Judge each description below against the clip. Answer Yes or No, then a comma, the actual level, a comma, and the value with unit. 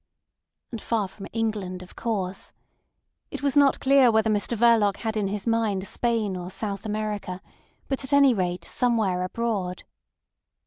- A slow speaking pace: No, average, 150 wpm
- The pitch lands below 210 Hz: No, high, 215 Hz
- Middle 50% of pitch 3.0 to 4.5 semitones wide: Yes, average, 3.4 semitones